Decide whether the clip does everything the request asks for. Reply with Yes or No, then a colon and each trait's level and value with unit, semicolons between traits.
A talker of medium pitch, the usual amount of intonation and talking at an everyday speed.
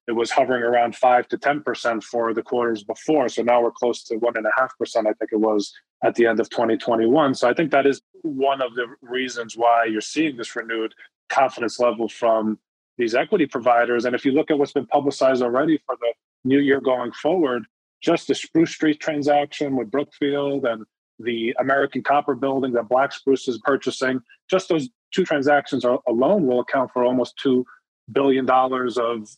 No: low, 130 Hz; average, 3.0 semitones; average, 190 wpm